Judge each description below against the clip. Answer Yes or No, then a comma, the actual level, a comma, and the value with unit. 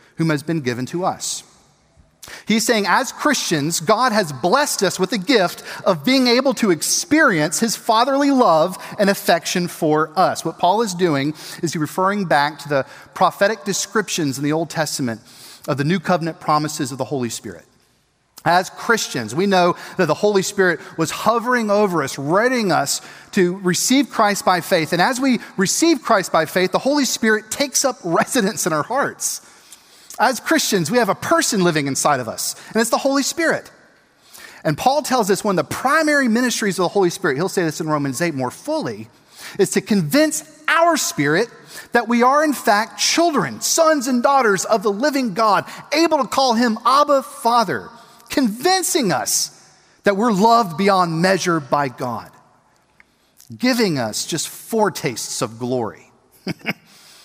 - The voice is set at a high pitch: Yes, high, 200 Hz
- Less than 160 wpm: No, average, 170 wpm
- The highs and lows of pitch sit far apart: Yes, wide, 7.2 semitones